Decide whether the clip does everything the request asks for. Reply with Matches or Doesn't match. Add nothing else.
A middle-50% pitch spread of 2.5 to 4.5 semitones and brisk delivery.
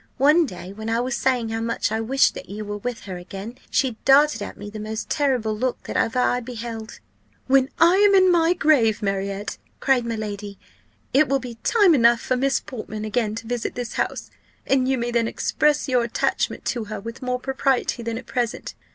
Matches